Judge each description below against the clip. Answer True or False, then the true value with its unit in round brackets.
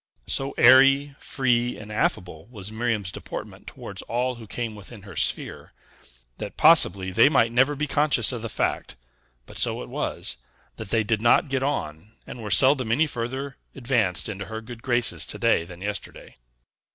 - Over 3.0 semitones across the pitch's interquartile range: True (4.2 semitones)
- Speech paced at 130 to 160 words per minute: False (175 wpm)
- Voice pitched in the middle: False (115 Hz)